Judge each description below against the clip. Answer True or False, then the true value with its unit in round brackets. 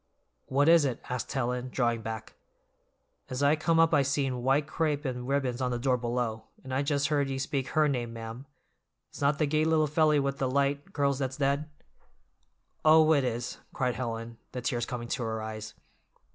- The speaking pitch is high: False (135 Hz)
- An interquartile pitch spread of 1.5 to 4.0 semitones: True (2.8 semitones)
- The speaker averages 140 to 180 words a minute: False (195 wpm)